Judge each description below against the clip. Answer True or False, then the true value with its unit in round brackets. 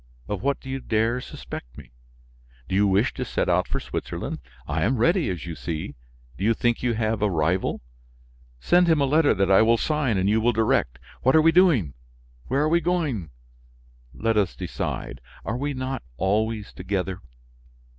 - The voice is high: False (110 Hz)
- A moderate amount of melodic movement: False (6.0 semitones)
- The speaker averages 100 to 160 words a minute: False (185 wpm)